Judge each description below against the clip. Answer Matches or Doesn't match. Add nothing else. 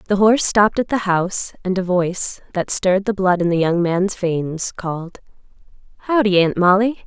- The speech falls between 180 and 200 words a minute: Matches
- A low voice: Doesn't match